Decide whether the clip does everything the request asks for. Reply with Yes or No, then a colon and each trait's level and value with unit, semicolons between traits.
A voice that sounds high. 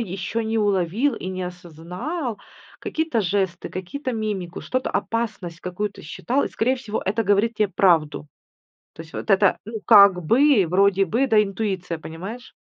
Yes: high, 200 Hz